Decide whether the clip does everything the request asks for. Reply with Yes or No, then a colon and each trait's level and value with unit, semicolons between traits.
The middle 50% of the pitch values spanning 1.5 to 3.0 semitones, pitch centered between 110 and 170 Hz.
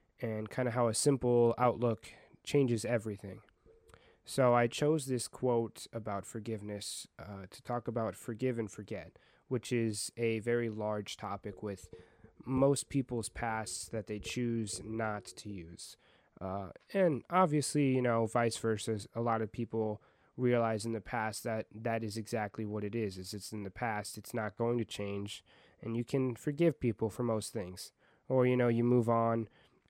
Yes: narrow, 2.4 semitones; low, 115 Hz